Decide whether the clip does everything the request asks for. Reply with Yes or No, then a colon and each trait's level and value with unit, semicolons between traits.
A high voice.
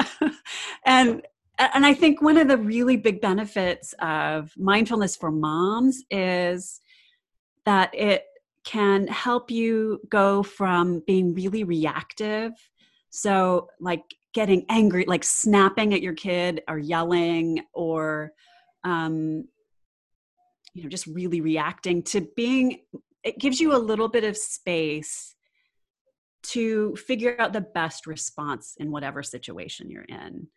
Yes: high, 200 Hz